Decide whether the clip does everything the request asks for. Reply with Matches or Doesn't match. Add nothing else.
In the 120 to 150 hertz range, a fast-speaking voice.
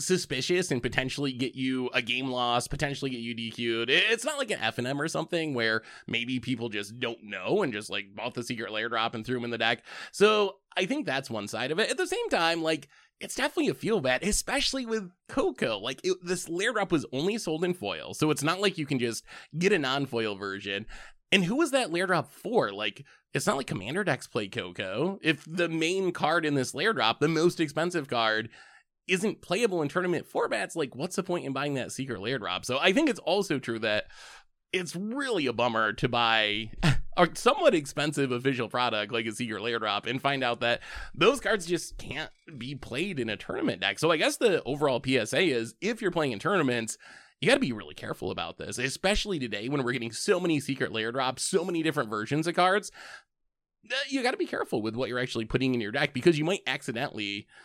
Matches